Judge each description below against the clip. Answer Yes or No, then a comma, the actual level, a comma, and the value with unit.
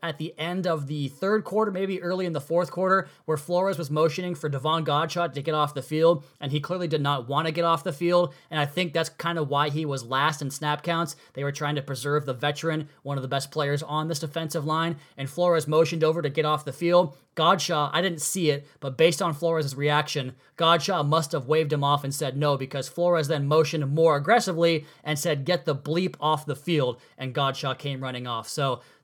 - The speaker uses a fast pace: Yes, fast, 235 wpm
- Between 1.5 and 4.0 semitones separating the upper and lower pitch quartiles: Yes, narrow, 2.6 semitones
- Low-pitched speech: No, medium, 155 Hz